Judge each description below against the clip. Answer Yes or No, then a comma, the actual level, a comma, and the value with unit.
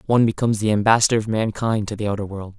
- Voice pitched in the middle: No, low, 110 Hz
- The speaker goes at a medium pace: No, fast, 230 wpm